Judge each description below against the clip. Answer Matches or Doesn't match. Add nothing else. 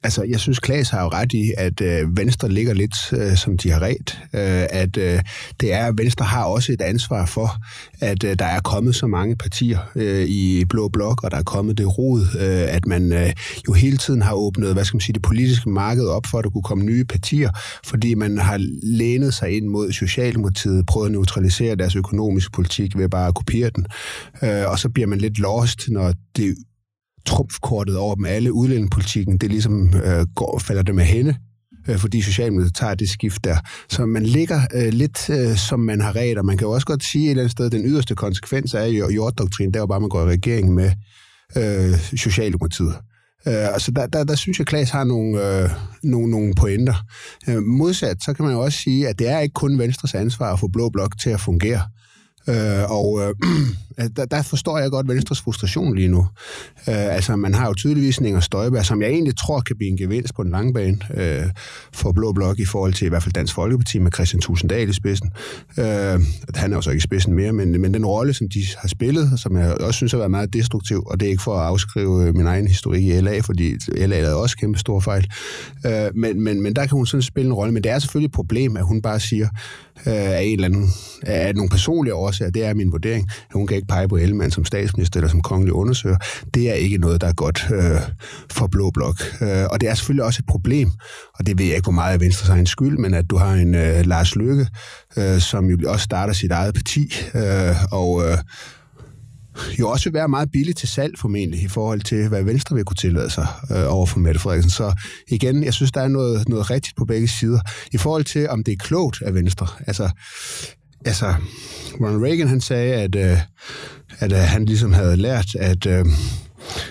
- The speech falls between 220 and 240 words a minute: Matches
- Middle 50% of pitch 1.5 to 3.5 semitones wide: Doesn't match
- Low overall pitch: Matches